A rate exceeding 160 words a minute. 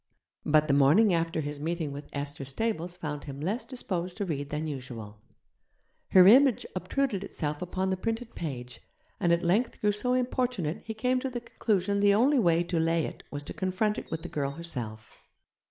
Yes: average, 190 wpm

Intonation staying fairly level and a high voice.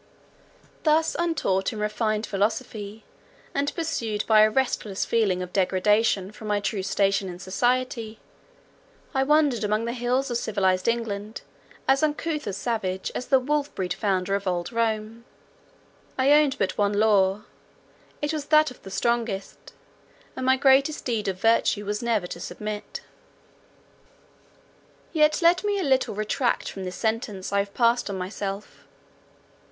No: average, 4.7 semitones; high, 220 Hz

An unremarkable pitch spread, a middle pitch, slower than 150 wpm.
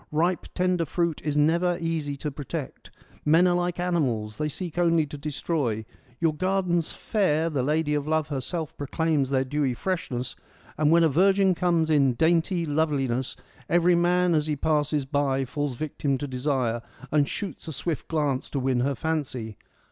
No: average, 3.5 semitones; medium, 155 Hz; average, 170 wpm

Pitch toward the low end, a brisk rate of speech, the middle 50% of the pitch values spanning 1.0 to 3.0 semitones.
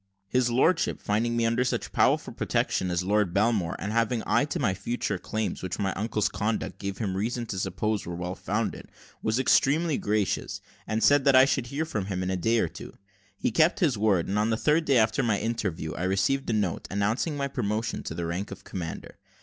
No: low, 110 Hz; fast, 220 wpm; average, 4.0 semitones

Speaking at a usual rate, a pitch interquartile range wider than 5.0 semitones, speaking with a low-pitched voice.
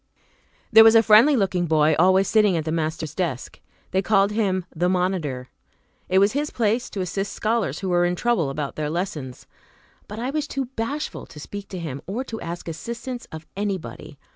No: average, 190 wpm; wide, 5.5 semitones; high, 190 Hz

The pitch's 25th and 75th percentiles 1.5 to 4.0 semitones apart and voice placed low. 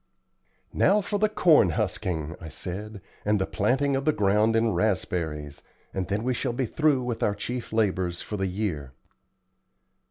No: wide, 5.5 semitones; low, 105 Hz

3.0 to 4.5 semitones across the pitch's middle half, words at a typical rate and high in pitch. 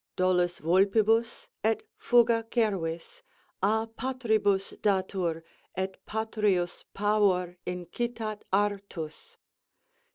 No: average, 3.5 semitones; slow, 75 wpm; high, 205 Hz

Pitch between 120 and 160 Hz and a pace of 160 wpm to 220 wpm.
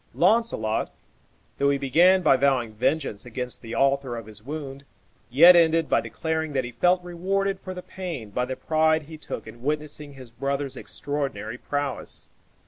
Yes: medium, 140 Hz; average, 165 wpm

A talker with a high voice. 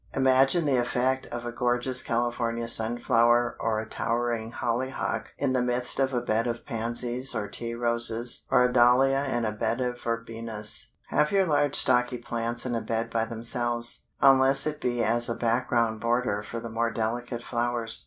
No: low, 120 Hz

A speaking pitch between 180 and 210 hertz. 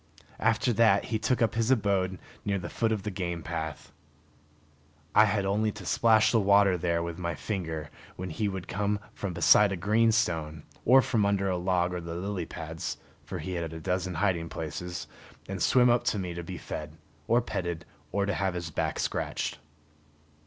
No: very low, 95 Hz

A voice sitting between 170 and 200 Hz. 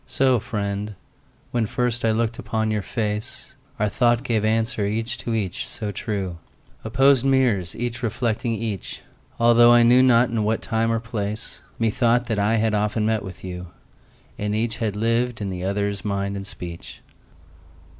No: low, 110 Hz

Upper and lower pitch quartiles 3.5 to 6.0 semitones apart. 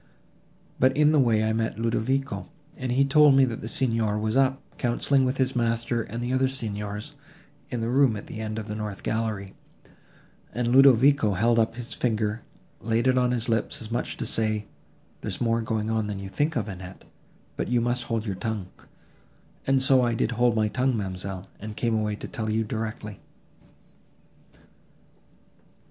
No: average, 2.9 semitones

